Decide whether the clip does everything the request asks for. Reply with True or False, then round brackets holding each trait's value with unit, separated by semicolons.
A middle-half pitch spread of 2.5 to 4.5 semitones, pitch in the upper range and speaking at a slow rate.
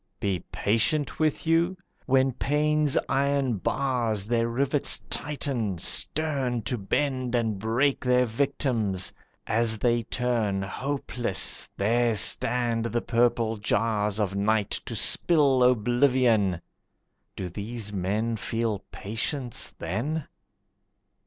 False (3.9 semitones; 120 Hz; 105 wpm)